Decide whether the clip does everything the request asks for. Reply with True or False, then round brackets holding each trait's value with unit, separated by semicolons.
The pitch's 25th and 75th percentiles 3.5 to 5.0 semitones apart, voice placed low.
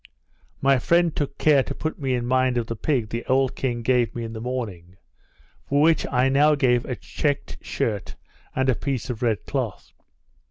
False (2.8 semitones; 130 Hz)